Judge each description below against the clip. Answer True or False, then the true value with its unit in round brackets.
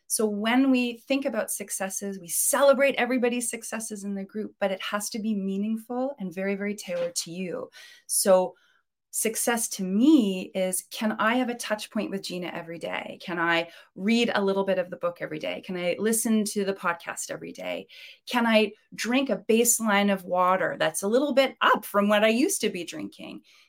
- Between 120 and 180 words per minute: False (200 wpm)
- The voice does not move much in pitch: False (4.1 semitones)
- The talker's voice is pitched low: False (210 Hz)